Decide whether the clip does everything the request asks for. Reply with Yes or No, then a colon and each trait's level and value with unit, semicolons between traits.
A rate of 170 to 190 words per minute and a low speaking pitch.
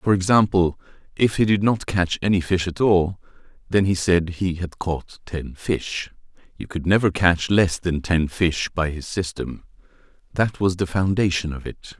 Yes: average, 175 wpm; very low, 90 Hz